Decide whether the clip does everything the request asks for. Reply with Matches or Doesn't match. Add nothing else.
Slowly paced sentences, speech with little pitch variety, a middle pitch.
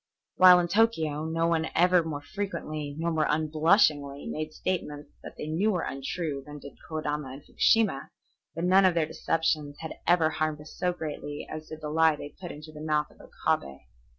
Doesn't match